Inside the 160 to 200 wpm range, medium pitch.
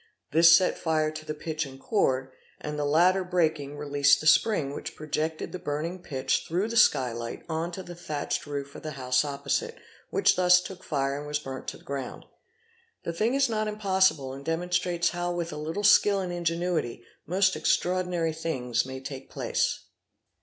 Yes: average, 185 wpm; medium, 160 Hz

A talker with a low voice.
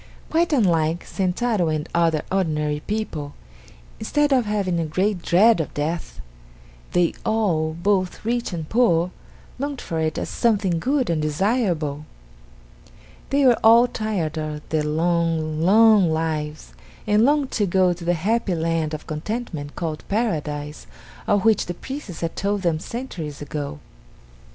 No: medium, 175 Hz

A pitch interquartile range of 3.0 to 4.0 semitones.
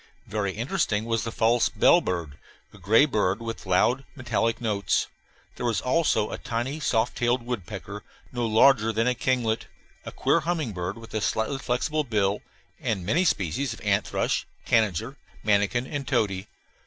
Yes: average, 3.5 semitones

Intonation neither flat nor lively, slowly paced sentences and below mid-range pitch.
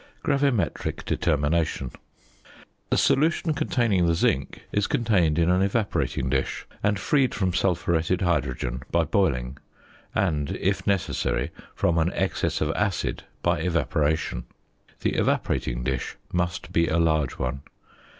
Yes: average, 4.9 semitones; slow, 125 wpm; very low, 85 Hz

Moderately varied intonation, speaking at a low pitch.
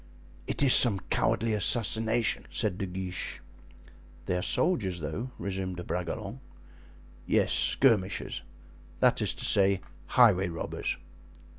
Yes: average, 3.9 semitones; low, 100 Hz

